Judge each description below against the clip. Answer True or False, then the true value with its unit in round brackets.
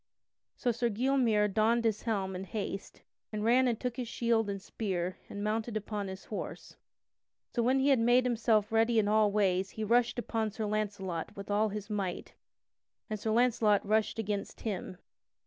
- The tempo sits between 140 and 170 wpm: False (180 wpm)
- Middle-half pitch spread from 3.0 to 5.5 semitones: False (2.4 semitones)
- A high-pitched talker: True (215 Hz)